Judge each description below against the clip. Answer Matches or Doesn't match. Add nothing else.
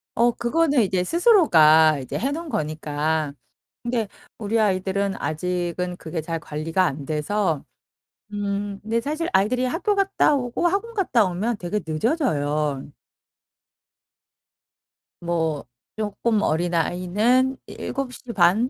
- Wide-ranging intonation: Matches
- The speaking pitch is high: Matches